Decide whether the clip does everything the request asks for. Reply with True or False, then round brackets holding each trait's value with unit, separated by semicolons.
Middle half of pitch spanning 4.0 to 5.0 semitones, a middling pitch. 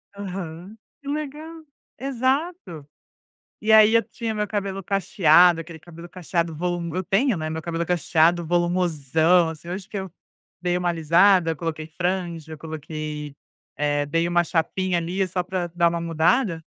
False (3.1 semitones; 175 Hz)